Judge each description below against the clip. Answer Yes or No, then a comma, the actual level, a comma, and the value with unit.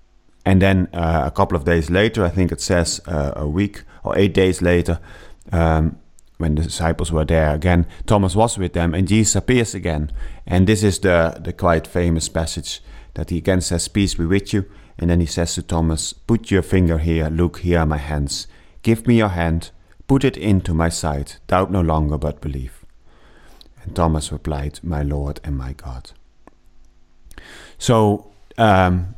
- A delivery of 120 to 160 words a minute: No, average, 185 wpm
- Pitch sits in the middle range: No, very low, 85 Hz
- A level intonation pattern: No, average, 3.0 semitones